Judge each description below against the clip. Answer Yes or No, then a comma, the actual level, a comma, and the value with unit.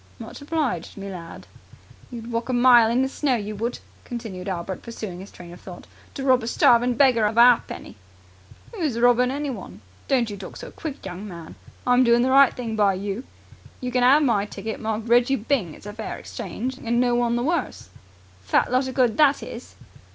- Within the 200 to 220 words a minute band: Yes, fast, 205 wpm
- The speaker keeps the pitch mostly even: No, average, 3.7 semitones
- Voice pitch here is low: No, high, 235 Hz